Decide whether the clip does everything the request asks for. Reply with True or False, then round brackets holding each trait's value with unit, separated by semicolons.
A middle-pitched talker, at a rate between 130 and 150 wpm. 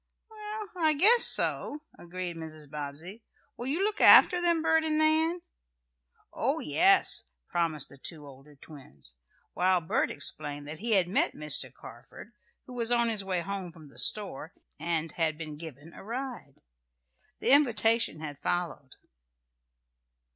True (180 Hz; 145 wpm)